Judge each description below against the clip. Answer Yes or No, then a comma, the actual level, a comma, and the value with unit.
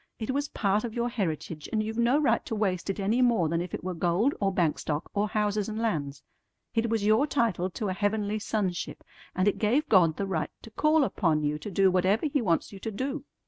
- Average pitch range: Yes, average, 4.0 semitones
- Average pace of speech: No, fast, 235 wpm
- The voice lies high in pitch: Yes, high, 205 Hz